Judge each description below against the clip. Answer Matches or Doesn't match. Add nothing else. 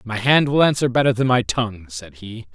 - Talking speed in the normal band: Doesn't match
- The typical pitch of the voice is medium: Doesn't match